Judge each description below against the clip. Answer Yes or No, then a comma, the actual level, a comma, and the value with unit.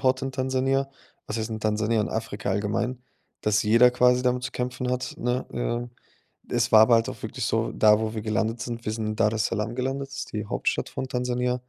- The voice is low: Yes, low, 120 Hz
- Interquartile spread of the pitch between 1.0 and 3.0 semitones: Yes, narrow, 2.5 semitones